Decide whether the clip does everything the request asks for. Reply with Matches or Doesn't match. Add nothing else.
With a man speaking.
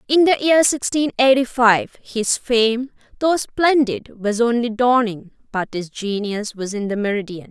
Doesn't match